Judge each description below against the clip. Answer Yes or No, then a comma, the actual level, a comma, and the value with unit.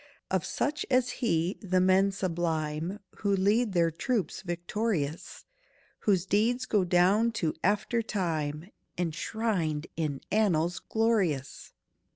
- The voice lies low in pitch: No, medium, 185 Hz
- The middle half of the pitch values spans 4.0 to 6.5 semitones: Yes, average, 4.6 semitones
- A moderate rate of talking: No, slow, 115 wpm